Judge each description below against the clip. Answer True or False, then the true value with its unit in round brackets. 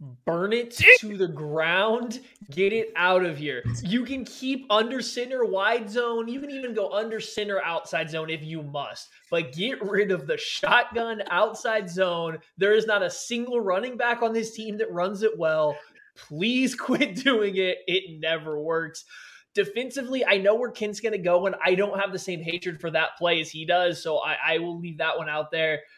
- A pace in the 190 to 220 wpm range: True (200 wpm)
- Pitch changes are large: True (5.9 semitones)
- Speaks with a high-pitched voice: True (200 Hz)